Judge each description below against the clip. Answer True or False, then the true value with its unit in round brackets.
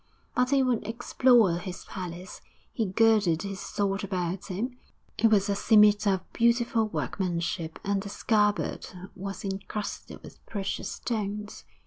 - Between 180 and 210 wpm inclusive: False (135 wpm)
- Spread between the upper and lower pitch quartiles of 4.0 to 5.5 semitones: False (2.9 semitones)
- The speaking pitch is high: True (200 Hz)